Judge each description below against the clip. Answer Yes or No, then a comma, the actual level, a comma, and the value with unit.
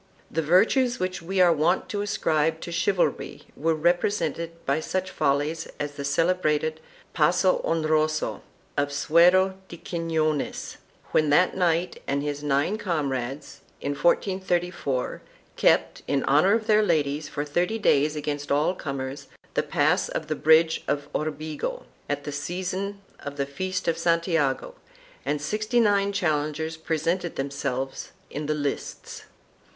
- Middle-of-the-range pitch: Yes, medium, 160 Hz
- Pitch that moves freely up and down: No, average, 3.9 semitones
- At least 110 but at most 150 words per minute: Yes, average, 140 wpm